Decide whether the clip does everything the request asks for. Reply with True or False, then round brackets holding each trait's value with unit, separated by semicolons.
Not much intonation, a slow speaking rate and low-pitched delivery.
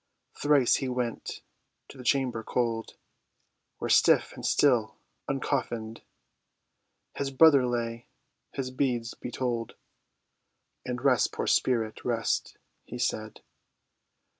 True (2.3 semitones; 110 wpm; 125 Hz)